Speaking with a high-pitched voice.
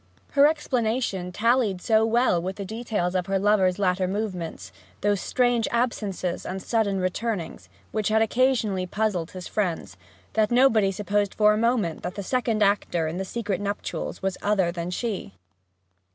Yes: high, 205 Hz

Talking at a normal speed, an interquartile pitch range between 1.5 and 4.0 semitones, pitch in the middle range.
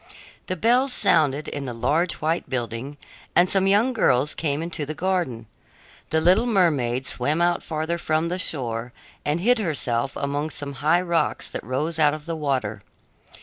No: average, 170 wpm; average, 4.6 semitones; medium, 155 Hz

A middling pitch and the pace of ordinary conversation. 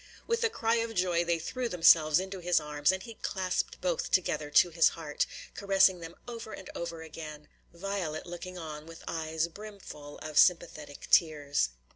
Yes: medium, 170 Hz; average, 170 wpm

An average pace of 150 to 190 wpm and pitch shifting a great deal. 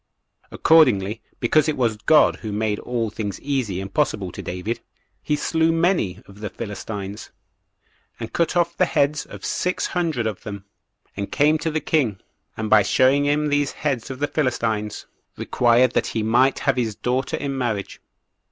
Yes: average, 170 wpm; wide, 5.7 semitones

